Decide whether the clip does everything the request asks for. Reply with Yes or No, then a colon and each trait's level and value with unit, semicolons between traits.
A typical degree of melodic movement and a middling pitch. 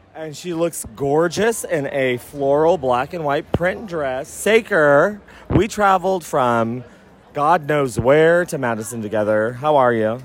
No: wide, 6.2 semitones; medium, 145 Hz